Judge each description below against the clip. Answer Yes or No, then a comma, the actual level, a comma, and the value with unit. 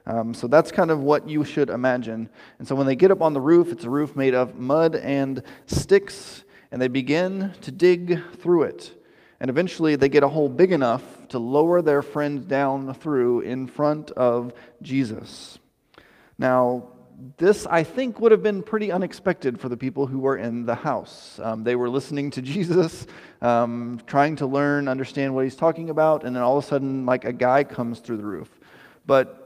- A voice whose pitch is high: No, medium, 140 Hz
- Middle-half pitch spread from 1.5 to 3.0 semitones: No, average, 4.3 semitones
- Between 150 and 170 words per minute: No, average, 200 wpm